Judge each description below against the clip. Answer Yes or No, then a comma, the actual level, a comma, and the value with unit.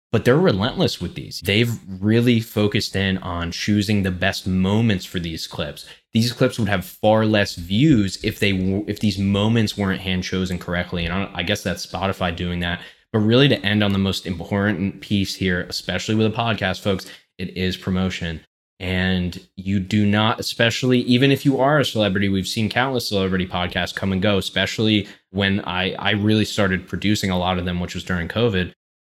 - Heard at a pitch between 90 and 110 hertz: Yes, very low, 95 Hz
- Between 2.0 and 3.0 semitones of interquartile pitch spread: Yes, narrow, 2.6 semitones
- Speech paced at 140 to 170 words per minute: No, average, 190 wpm